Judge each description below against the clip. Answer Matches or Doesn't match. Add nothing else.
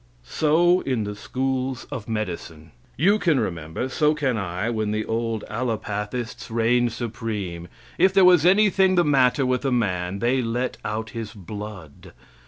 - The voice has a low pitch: Matches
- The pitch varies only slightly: Doesn't match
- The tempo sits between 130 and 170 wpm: Matches